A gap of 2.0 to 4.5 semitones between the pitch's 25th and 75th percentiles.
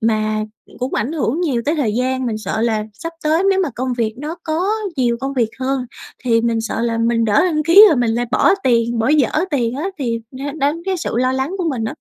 No: average, 4.9 semitones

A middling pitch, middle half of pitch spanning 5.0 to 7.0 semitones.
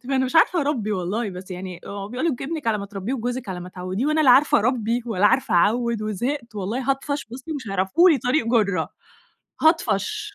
No: high, 235 Hz; wide, 5.5 semitones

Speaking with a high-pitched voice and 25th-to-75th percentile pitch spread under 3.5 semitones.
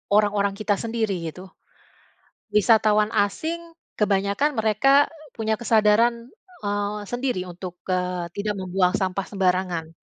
Yes: high, 205 Hz; average, 3.1 semitones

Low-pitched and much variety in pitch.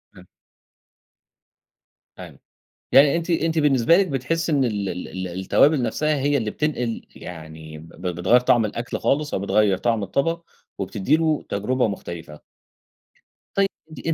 Yes: low, 125 Hz; wide, 7.8 semitones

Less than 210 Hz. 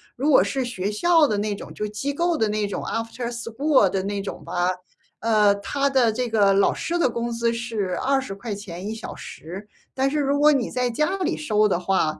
No: high, 230 Hz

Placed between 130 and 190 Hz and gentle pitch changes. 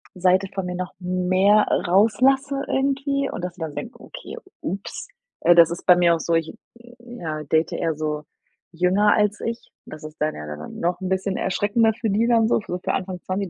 No: medium, 185 Hz; average, 4.7 semitones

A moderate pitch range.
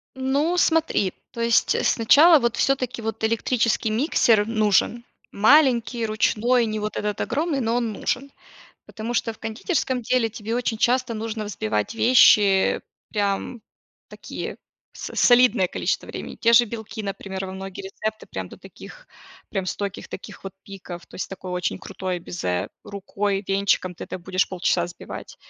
Yes: average, 3.8 semitones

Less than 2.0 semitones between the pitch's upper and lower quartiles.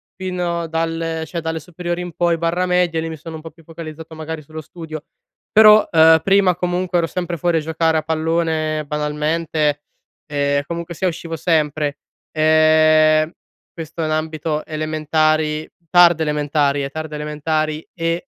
Yes: narrow, 1.5 semitones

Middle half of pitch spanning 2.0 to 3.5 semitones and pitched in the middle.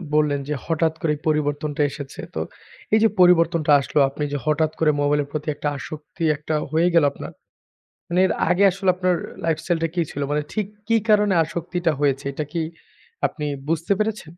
Yes: average, 2.9 semitones; medium, 160 Hz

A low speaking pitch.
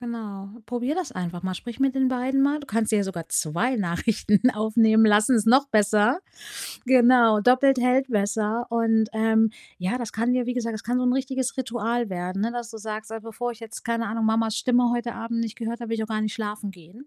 No: high, 230 Hz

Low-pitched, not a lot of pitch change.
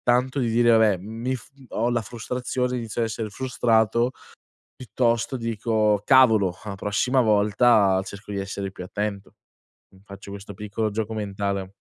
No: low, 110 Hz; average, 3.0 semitones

